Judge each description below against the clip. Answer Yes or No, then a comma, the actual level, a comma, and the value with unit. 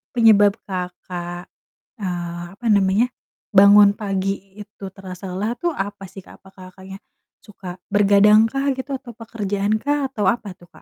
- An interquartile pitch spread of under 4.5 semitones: Yes, narrow, 2.6 semitones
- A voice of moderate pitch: No, high, 200 Hz